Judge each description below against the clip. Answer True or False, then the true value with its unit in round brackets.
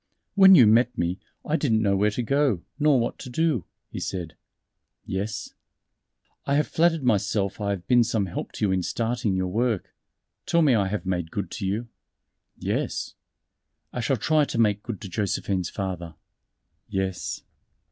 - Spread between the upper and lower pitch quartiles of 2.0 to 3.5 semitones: False (4.7 semitones)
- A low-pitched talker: True (105 Hz)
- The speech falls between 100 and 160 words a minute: False (170 wpm)